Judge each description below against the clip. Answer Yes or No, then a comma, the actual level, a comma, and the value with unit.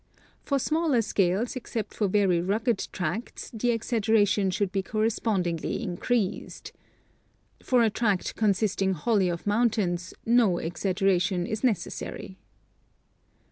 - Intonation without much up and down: No, average, 3.5 semitones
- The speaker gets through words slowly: Yes, slow, 115 wpm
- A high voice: Yes, high, 205 Hz